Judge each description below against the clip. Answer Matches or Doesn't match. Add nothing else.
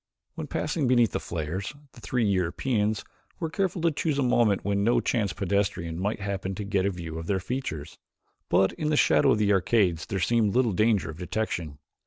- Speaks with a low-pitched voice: Matches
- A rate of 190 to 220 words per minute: Matches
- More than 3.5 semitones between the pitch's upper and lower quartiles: Matches